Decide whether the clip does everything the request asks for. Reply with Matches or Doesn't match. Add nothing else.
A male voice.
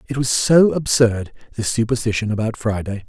Matches